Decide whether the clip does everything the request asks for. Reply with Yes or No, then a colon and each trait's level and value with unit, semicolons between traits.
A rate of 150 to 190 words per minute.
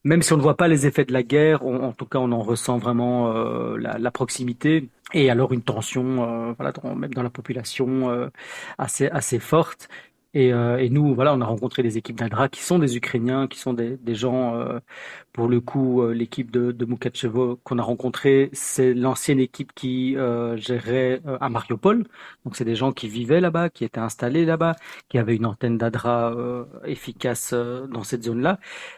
No: average, 210 wpm